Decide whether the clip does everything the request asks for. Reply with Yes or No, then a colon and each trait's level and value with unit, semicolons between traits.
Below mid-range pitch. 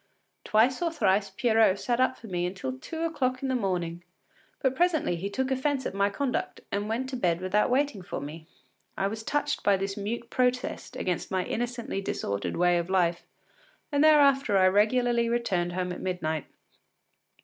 No: high, 210 Hz